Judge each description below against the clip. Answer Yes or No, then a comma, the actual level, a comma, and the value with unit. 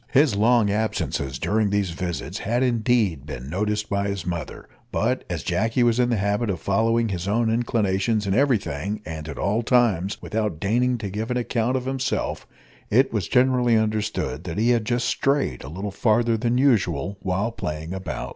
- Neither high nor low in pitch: No, low, 105 Hz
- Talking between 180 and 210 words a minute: Yes, average, 185 wpm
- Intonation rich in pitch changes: No, average, 3.9 semitones